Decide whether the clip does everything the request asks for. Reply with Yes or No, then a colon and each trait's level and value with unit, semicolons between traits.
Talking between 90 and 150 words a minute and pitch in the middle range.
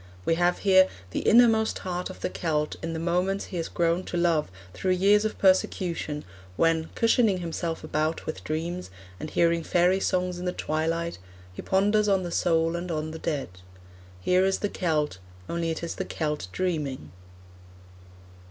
No: average, 170 wpm; medium, 170 Hz